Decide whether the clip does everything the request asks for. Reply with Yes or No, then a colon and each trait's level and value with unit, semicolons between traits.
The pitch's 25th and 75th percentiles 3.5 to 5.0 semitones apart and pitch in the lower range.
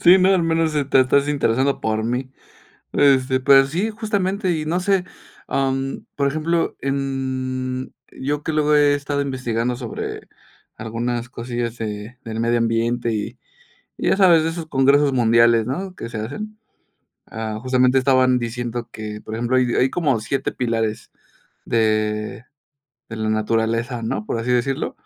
Yes: average, 3.8 semitones; low, 130 Hz